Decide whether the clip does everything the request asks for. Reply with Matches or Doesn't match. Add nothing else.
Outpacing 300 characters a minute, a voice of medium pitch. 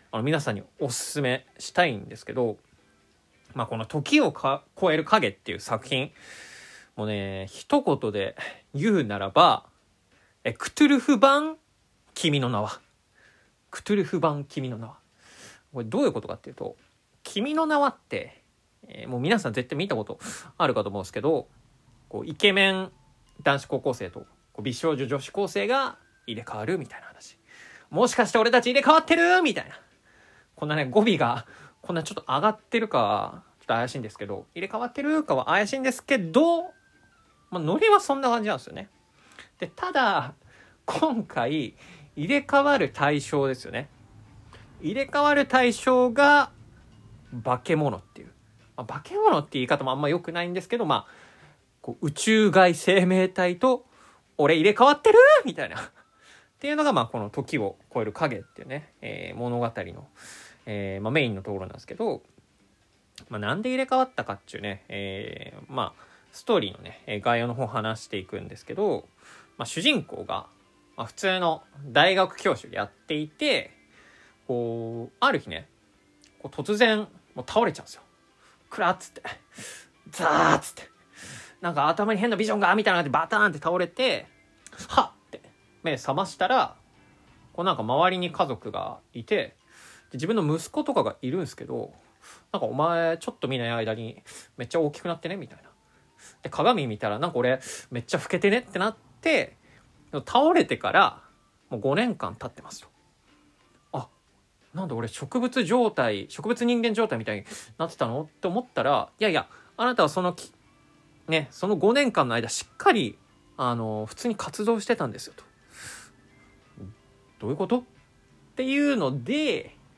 Matches